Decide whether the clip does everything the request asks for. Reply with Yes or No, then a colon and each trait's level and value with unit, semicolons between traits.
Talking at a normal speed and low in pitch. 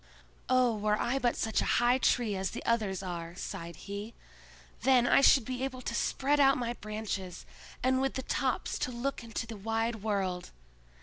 No: average, 185 wpm; high, 230 Hz